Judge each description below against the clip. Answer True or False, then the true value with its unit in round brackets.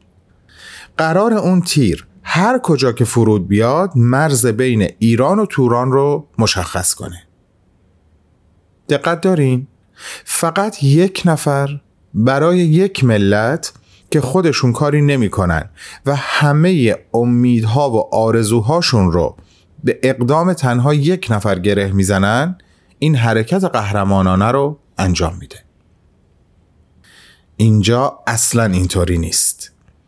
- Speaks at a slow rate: True (100 wpm)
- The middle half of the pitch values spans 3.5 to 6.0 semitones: False (7.2 semitones)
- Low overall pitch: True (120 Hz)